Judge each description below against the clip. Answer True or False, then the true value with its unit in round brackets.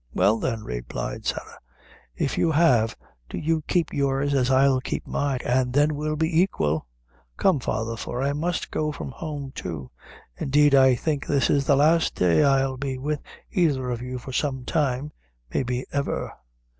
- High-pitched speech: False (135 Hz)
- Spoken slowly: False (170 wpm)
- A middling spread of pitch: True (3.0 semitones)